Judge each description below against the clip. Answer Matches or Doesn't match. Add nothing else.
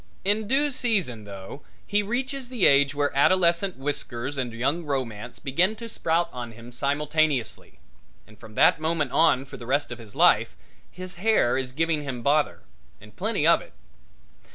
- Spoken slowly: Doesn't match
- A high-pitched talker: Doesn't match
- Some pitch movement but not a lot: Doesn't match